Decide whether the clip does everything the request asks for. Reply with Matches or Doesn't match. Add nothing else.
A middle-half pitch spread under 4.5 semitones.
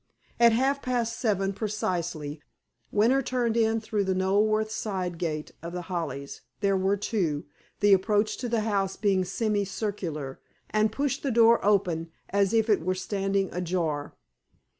Matches